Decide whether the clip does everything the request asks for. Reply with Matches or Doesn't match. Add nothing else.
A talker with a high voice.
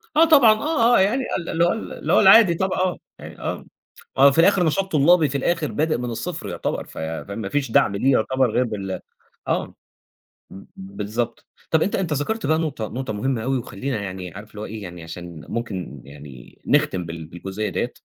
Doesn't match